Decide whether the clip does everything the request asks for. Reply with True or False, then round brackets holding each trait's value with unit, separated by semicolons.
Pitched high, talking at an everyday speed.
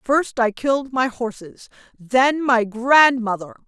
False (245 Hz; 130 wpm)